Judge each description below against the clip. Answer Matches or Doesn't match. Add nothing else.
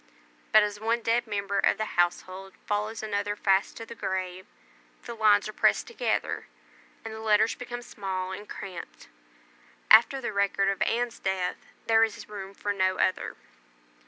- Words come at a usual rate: Matches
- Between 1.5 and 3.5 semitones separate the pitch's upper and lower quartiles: Matches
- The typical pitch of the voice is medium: Doesn't match